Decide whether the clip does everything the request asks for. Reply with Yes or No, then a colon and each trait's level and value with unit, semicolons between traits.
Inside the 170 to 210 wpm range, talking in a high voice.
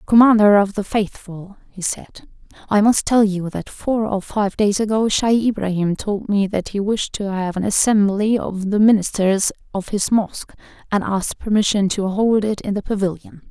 Yes: average, 185 wpm; high, 205 Hz